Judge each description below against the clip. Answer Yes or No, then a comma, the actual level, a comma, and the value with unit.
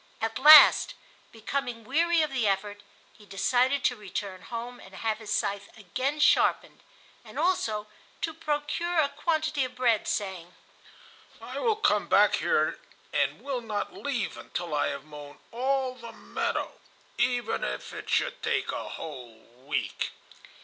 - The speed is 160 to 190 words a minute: No, average, 150 wpm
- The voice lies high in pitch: Yes, high, 240 Hz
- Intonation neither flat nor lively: No, wide, 5.9 semitones